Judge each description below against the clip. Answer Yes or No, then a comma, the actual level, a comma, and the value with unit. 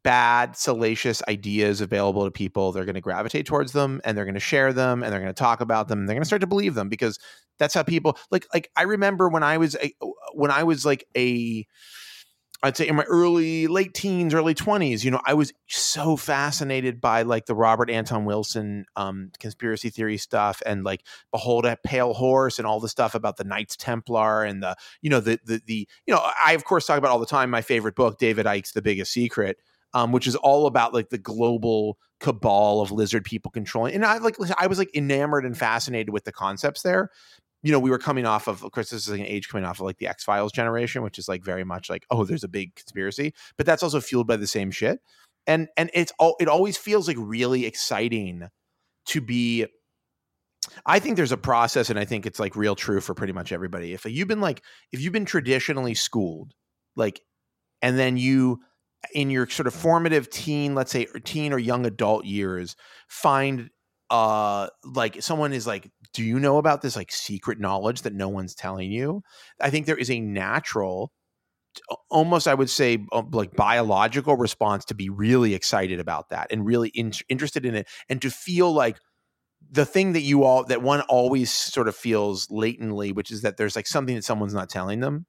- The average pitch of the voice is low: Yes, low, 120 Hz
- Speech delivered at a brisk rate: Yes, fast, 215 wpm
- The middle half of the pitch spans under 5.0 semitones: No, wide, 5.4 semitones